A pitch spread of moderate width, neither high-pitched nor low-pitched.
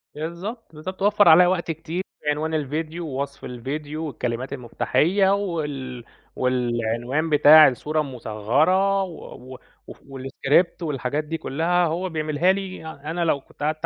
Yes: average, 4.3 semitones; medium, 155 Hz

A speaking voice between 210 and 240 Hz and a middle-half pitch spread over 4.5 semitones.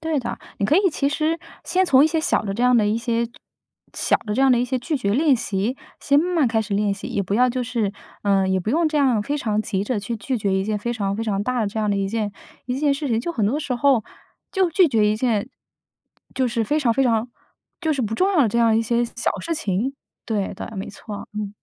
Yes: high, 235 Hz; average, 5.0 semitones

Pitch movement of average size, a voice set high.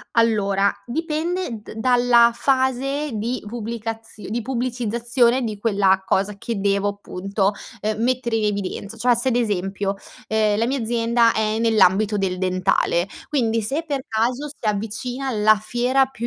Yes: average, 3.1 semitones; high, 225 Hz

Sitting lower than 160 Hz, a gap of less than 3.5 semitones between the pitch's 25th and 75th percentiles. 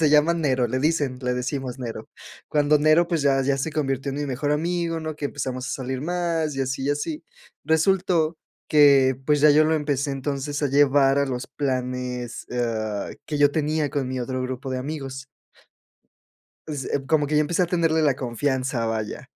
Yes: medium, 140 Hz; average, 2.9 semitones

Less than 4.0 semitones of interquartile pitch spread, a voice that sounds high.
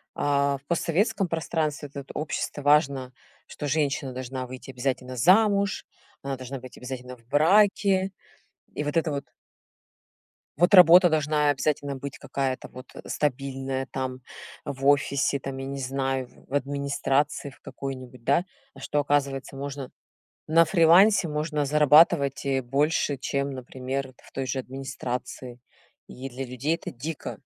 No: narrow, 2.4 semitones; medium, 140 Hz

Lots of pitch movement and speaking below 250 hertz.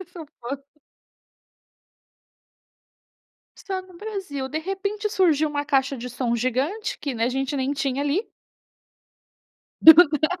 No: wide, 5.8 semitones; very high, 290 Hz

